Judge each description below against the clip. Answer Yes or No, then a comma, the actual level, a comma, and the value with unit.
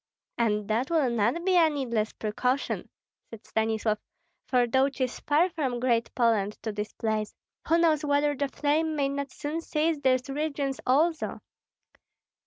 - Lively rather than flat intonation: No, average, 4.7 semitones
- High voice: Yes, very high, 270 Hz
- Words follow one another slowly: No, average, 155 wpm